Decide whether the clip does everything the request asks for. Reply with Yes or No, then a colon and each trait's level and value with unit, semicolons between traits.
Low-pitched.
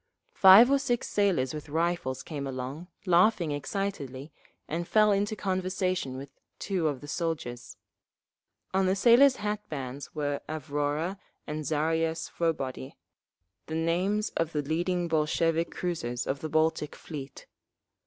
No: medium, 160 Hz